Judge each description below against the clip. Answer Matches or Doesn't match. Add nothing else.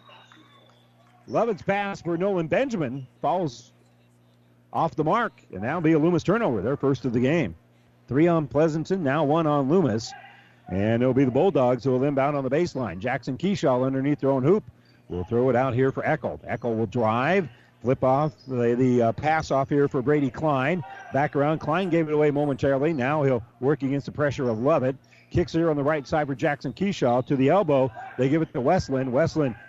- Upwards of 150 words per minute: Matches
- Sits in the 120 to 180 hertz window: Matches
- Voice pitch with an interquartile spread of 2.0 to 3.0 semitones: Doesn't match